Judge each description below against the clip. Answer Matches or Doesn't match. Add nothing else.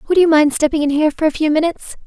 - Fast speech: Matches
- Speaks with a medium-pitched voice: Doesn't match